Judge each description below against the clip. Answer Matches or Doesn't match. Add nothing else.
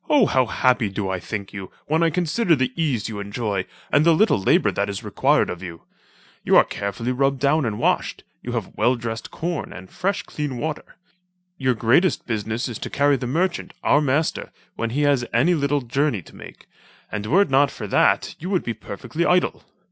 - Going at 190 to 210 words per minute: Matches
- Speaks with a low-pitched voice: Matches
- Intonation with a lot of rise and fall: Matches